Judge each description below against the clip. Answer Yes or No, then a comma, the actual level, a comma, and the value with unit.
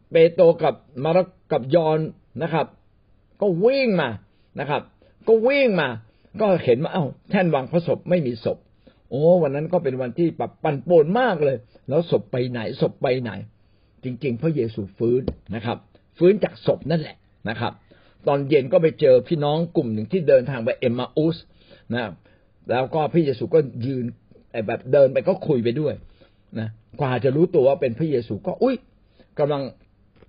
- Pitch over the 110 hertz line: Yes, low, 135 Hz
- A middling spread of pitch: No, wide, 7.2 semitones